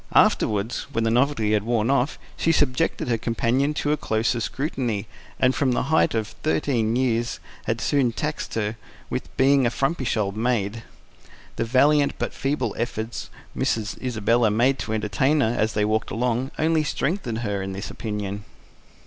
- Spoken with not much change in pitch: No, average, 3.8 semitones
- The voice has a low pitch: Yes, low, 120 Hz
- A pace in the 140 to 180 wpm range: Yes, average, 165 wpm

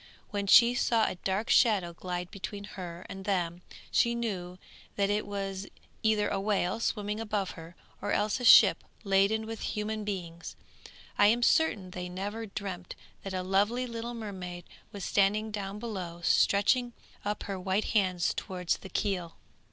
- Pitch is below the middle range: No, high, 200 Hz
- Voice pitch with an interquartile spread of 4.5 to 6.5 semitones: No, average, 2.7 semitones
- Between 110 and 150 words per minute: No, average, 160 wpm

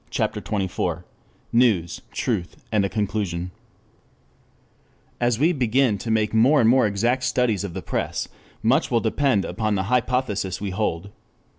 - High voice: No, low, 110 Hz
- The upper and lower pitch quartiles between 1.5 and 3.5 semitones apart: No, average, 4.1 semitones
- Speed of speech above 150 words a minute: No, average, 145 wpm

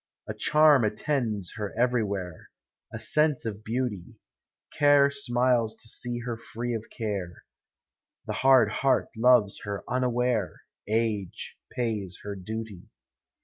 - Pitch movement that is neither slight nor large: Yes, average, 3.3 semitones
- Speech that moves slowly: Yes, slow, 125 wpm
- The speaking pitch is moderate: No, low, 115 Hz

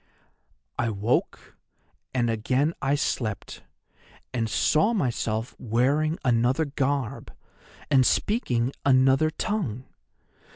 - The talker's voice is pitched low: Yes, low, 130 Hz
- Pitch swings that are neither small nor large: Yes, average, 3.7 semitones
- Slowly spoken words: Yes, slow, 90 wpm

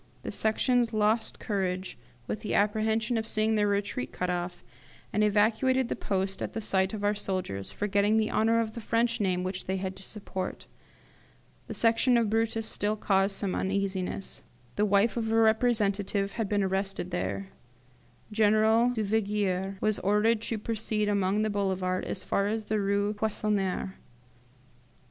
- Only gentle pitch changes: Yes, narrow, 2.3 semitones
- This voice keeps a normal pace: Yes, average, 160 wpm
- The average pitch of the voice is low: No, high, 210 Hz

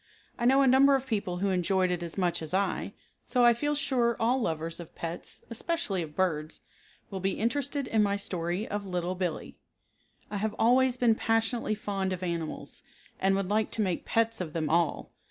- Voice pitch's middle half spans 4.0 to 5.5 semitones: Yes, average, 4.9 semitones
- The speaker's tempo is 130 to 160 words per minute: No, average, 195 wpm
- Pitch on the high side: Yes, high, 200 Hz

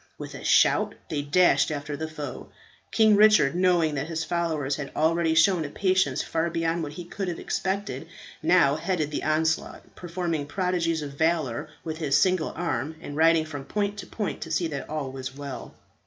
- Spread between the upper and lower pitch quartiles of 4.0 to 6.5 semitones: No, average, 3.3 semitones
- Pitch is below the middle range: No, medium, 160 Hz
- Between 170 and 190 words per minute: Yes, average, 185 wpm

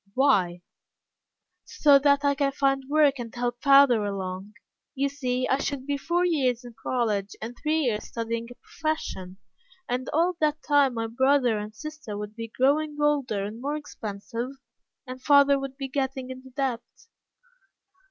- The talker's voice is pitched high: Yes, very high, 260 Hz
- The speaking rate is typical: Yes, average, 160 wpm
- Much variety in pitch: No, average, 3.7 semitones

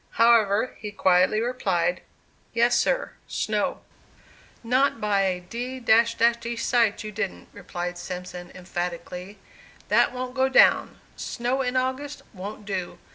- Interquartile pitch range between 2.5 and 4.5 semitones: No, average, 5.1 semitones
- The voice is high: Yes, high, 220 Hz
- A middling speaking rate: No, slow, 125 wpm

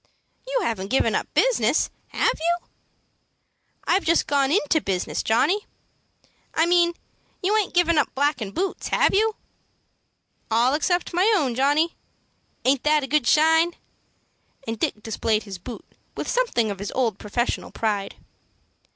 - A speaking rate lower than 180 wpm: Yes, average, 140 wpm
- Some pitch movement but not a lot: No, wide, 7.3 semitones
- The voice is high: Yes, very high, 295 Hz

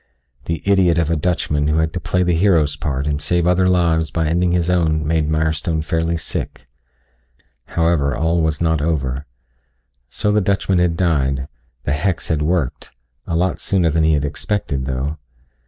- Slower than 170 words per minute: No, average, 175 wpm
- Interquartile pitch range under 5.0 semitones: Yes, average, 2.8 semitones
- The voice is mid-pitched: No, very low, 80 Hz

